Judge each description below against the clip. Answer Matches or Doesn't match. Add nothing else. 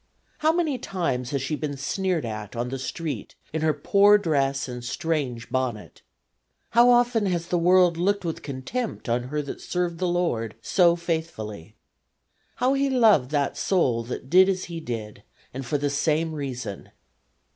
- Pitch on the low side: Doesn't match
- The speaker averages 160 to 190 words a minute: Matches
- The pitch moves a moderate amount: Doesn't match